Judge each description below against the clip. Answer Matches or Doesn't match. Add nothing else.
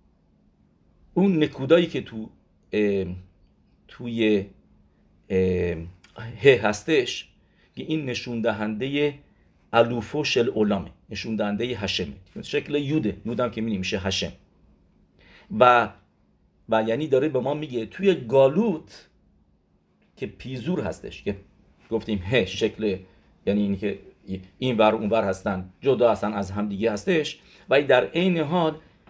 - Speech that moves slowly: Matches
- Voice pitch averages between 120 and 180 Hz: Doesn't match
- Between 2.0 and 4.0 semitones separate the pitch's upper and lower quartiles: Doesn't match